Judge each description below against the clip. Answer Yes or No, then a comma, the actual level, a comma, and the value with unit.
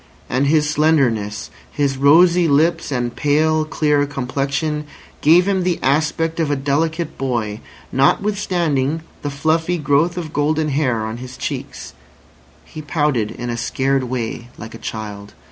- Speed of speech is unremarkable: Yes, average, 145 wpm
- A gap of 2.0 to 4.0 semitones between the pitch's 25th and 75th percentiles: Yes, average, 3.7 semitones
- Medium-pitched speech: Yes, medium, 145 Hz